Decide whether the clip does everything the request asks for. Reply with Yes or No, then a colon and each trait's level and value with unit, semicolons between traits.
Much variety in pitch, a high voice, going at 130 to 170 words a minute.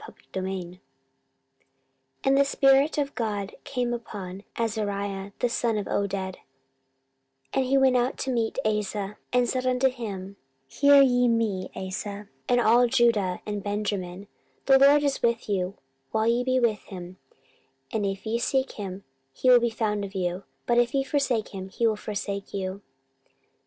No: average, 4.0 semitones; high, 220 Hz; average, 160 wpm